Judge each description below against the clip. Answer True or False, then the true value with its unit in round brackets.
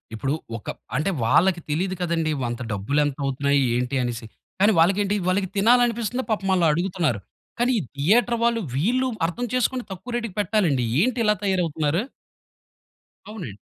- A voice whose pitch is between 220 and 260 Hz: False (185 Hz)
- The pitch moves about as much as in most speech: False (7.1 semitones)